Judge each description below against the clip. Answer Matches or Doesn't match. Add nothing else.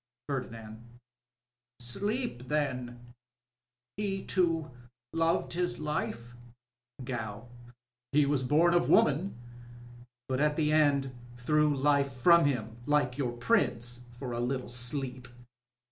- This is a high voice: Doesn't match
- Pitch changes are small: Doesn't match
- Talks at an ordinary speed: Doesn't match